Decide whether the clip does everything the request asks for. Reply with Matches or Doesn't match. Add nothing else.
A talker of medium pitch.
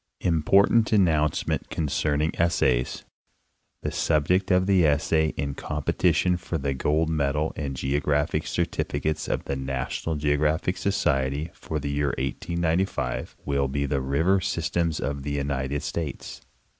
Doesn't match